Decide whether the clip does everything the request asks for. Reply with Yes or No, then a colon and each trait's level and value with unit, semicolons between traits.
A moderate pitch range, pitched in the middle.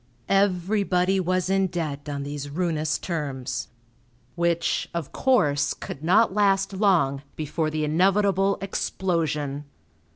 Yes: average, 4.5 semitones; medium, 170 Hz